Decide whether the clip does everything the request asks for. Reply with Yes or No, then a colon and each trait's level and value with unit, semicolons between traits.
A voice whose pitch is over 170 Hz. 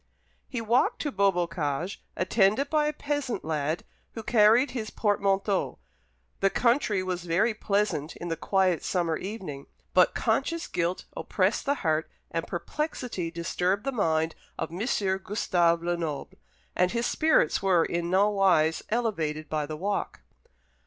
Yes: high, 190 Hz